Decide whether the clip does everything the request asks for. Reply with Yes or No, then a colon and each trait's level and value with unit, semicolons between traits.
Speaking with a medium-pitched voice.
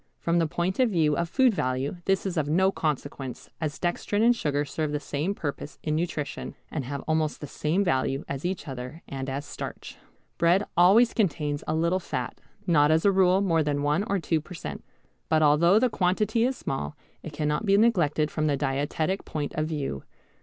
Yes: medium, 155 Hz